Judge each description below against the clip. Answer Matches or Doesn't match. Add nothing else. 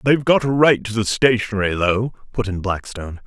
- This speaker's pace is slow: Doesn't match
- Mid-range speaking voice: Doesn't match